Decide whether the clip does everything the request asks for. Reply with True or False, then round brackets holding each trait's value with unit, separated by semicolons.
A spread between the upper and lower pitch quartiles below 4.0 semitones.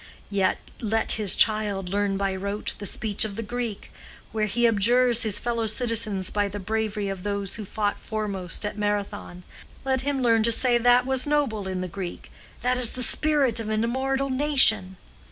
True (3.3 semitones)